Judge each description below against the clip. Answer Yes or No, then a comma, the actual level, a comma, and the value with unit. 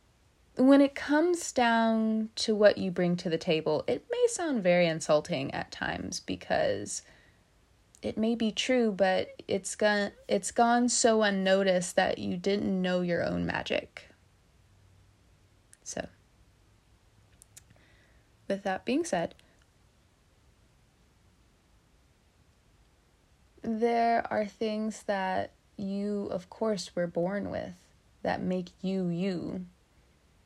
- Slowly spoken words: Yes, slow, 110 wpm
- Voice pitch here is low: No, medium, 185 Hz